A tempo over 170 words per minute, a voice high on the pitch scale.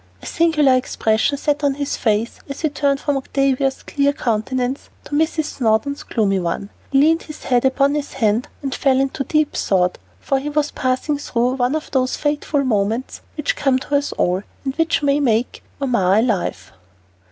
Yes: average, 185 wpm; very high, 270 Hz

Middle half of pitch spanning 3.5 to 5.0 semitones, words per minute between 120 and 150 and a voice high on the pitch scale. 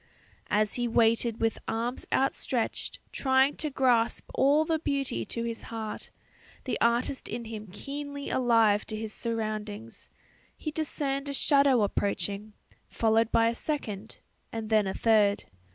Yes: average, 3.9 semitones; average, 140 wpm; high, 230 Hz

